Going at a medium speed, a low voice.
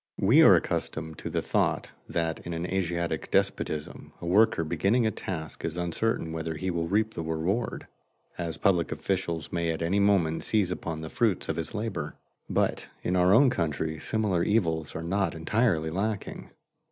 Yes: average, 175 wpm; very low, 85 Hz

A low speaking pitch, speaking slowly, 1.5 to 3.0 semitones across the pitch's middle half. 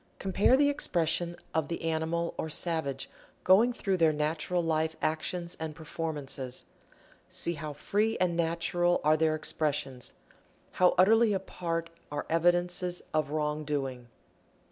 No: medium, 165 Hz; slow, 130 wpm; narrow, 2.5 semitones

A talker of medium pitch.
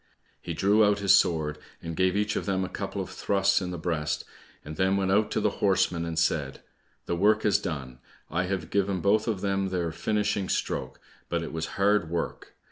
No: very low, 95 Hz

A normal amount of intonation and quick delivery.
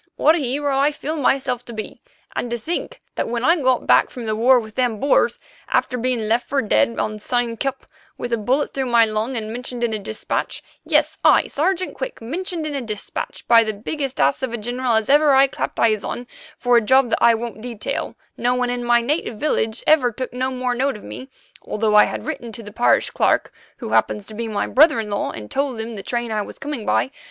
Yes: average, 3.4 semitones; fast, 230 wpm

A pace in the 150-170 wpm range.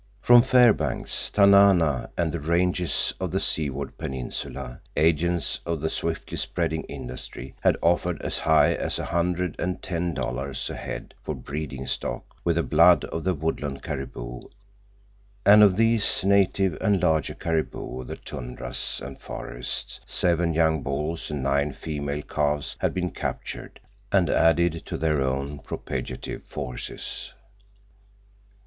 No: average, 140 wpm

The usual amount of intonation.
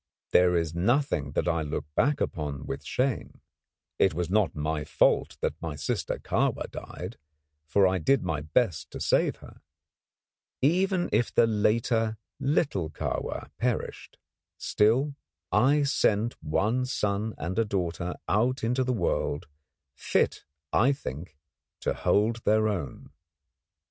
No: wide, 7.0 semitones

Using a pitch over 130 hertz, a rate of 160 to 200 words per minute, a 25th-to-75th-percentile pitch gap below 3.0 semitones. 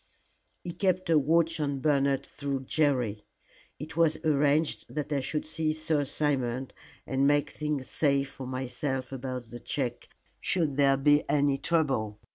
No: medium, 140 Hz; average, 150 wpm; narrow, 2.6 semitones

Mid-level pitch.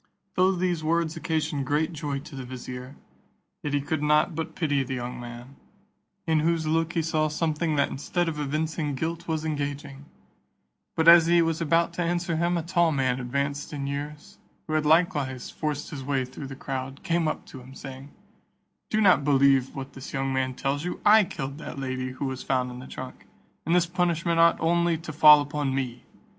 Yes: medium, 150 Hz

